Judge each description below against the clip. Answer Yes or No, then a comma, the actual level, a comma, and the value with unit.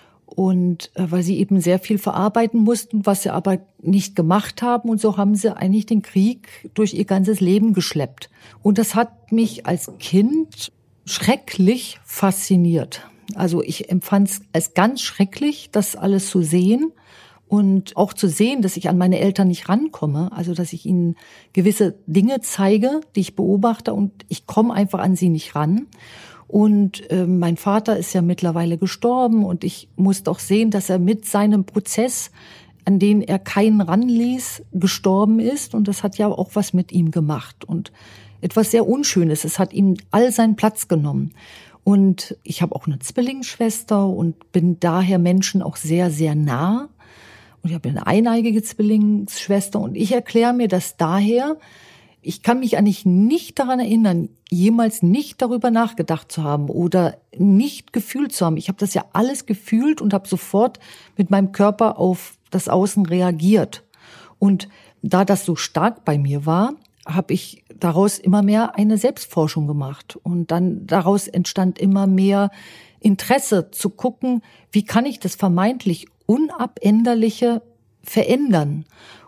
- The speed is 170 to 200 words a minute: No, average, 160 wpm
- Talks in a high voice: Yes, high, 195 Hz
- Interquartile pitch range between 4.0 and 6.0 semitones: No, average, 3.4 semitones